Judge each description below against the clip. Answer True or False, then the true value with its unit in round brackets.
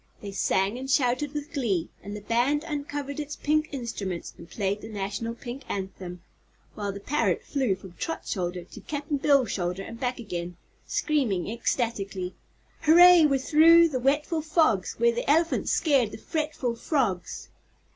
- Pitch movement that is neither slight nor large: False (6.9 semitones)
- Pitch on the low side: False (245 Hz)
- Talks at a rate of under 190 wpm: True (160 wpm)